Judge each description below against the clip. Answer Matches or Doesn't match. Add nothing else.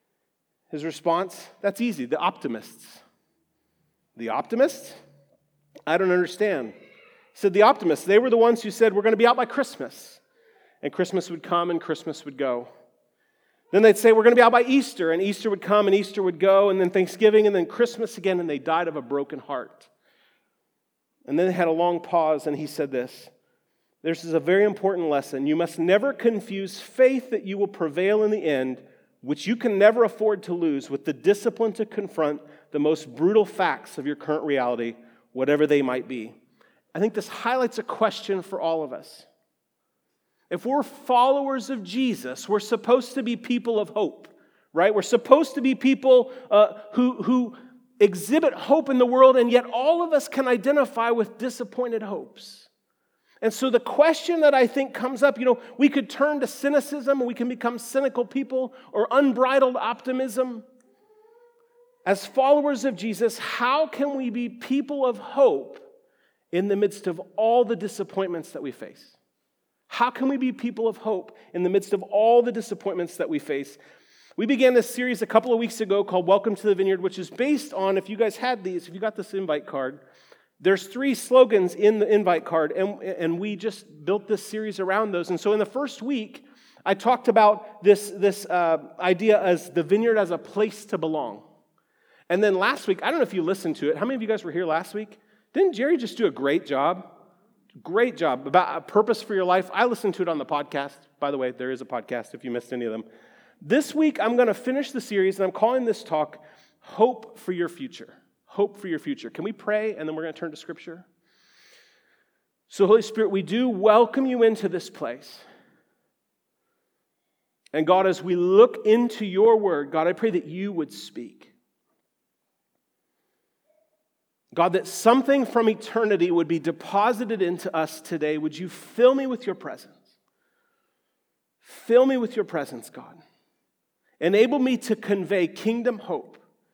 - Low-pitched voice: Doesn't match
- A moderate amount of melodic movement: Doesn't match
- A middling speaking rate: Matches